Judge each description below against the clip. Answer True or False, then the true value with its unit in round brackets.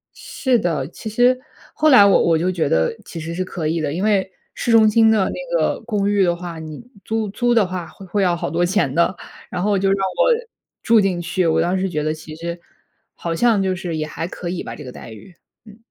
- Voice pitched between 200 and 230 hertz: False (185 Hz)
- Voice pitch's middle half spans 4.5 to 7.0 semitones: False (3.9 semitones)